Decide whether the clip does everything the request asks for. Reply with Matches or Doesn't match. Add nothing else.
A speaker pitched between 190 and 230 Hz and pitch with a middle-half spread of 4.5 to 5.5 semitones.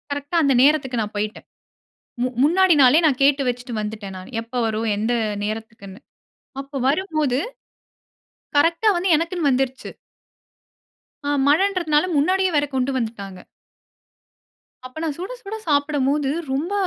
Doesn't match